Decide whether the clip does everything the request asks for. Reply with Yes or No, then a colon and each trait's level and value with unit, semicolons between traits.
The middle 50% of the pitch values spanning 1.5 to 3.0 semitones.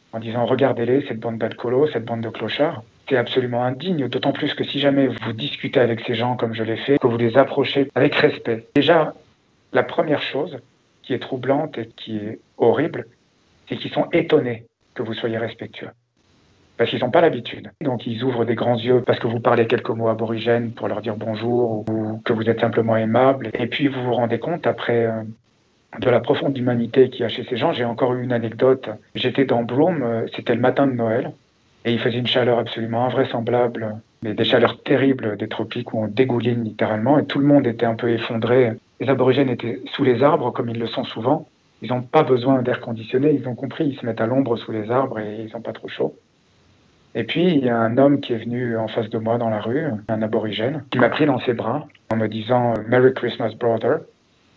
Yes: narrow, 2.5 semitones